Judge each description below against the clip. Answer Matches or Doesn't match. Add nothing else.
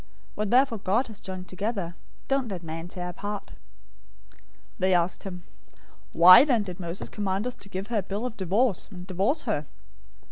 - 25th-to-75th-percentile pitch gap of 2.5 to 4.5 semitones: Matches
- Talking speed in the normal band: Matches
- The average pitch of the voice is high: Matches